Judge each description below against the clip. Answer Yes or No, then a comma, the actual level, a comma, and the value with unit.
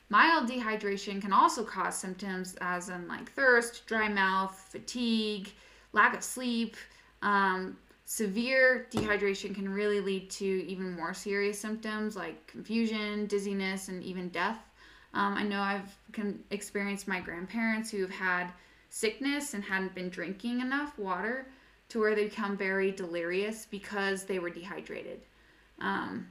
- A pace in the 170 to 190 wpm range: No, average, 140 wpm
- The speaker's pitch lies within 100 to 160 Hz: No, high, 200 Hz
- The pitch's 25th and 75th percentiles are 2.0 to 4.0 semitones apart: Yes, narrow, 2.5 semitones